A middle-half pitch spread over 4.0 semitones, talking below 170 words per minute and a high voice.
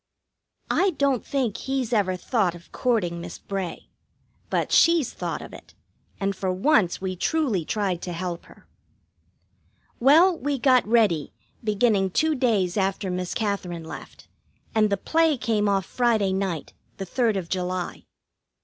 Yes: average, 5.3 semitones; average, 150 wpm; high, 200 Hz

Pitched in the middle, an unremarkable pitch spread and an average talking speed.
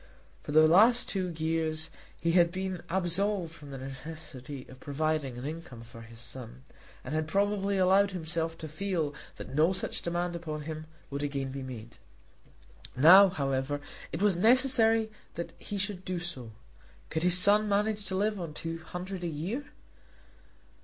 Yes: medium, 165 Hz; average, 4.6 semitones; average, 165 wpm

